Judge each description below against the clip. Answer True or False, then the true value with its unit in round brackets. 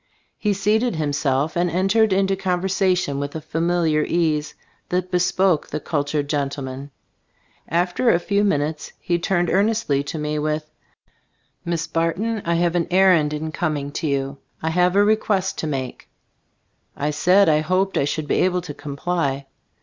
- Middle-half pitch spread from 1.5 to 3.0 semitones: False (3.8 semitones)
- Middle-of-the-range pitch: True (170 Hz)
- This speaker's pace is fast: False (155 wpm)